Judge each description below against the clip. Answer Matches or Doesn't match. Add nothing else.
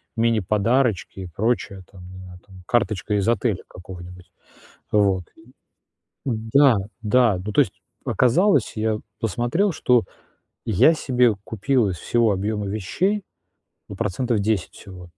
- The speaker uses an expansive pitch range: Doesn't match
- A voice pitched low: Matches